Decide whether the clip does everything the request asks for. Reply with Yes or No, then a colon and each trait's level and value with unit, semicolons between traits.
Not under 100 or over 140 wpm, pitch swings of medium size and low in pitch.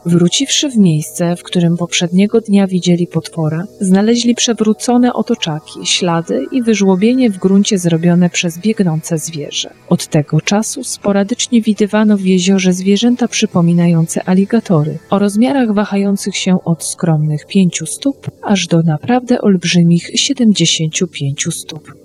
No: average, 125 wpm; average, 4.2 semitones; high, 190 Hz